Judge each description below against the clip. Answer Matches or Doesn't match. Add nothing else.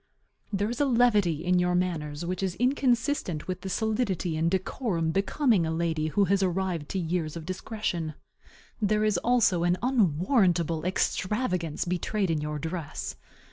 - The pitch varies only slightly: Doesn't match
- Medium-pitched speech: Matches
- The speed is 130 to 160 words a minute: Matches